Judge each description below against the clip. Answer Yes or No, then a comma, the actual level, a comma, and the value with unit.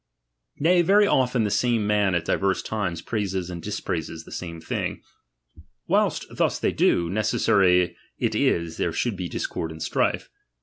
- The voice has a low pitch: Yes, very low, 95 Hz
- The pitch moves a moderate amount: Yes, average, 4.2 semitones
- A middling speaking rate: Yes, average, 160 wpm